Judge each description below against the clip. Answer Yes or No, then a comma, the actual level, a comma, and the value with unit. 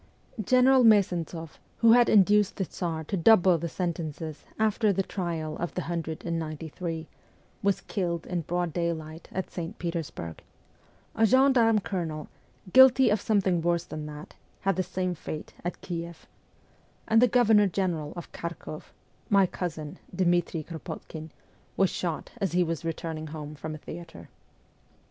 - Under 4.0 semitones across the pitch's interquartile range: Yes, average, 3.6 semitones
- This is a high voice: No, medium, 175 Hz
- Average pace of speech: Yes, average, 155 wpm